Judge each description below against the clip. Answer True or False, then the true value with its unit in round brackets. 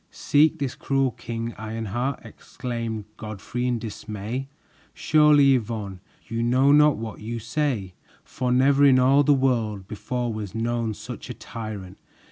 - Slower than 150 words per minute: True (140 wpm)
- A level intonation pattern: False (3.7 semitones)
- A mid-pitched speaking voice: False (120 Hz)